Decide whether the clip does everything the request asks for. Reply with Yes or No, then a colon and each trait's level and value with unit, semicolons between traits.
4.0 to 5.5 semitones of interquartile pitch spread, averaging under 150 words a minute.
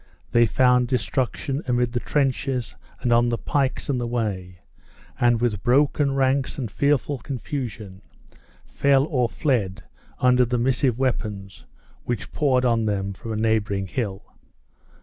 No: average, 3.3 semitones; average, 140 wpm